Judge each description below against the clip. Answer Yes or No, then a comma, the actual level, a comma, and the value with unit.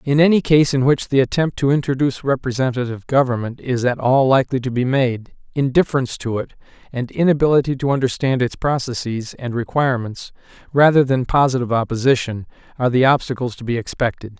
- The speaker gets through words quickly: No, average, 165 wpm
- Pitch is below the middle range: Yes, low, 130 Hz